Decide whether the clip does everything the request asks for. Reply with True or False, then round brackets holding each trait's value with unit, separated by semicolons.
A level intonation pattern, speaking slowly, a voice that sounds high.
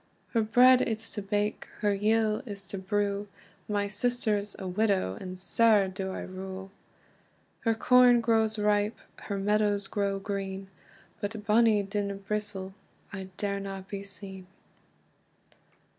True (1.7 semitones; 130 wpm; 205 Hz)